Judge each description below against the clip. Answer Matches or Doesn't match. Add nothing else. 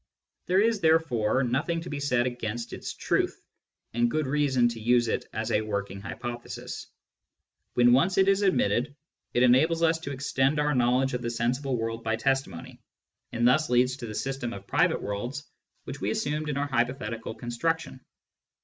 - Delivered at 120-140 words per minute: Doesn't match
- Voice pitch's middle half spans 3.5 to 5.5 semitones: Matches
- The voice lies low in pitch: Matches